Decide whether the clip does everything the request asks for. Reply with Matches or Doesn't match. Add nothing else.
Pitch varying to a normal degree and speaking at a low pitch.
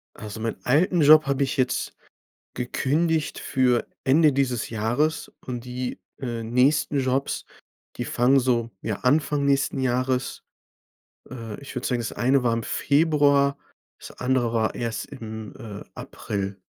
Matches